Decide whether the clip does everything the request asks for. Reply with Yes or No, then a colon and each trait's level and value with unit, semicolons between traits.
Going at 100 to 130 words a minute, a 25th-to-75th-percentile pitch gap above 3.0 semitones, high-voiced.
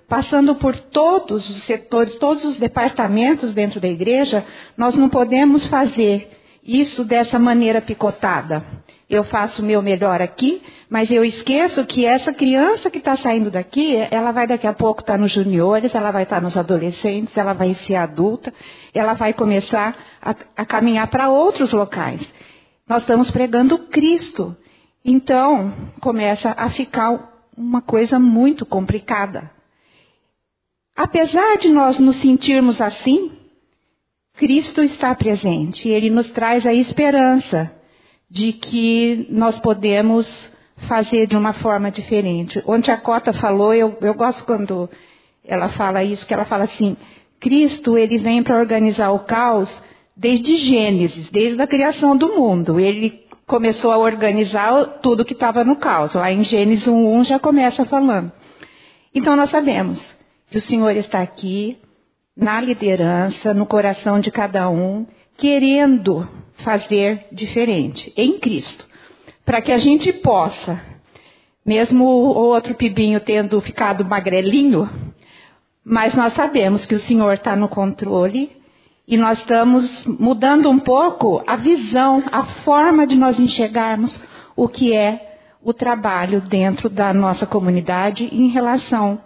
No: average, 140 wpm; average, 3.8 semitones; high, 230 Hz